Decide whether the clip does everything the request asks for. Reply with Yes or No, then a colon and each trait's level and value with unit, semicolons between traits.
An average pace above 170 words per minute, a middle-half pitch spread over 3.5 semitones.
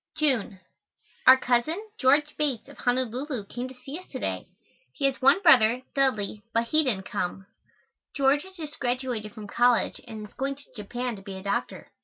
Yes: average, 185 wpm; average, 4.1 semitones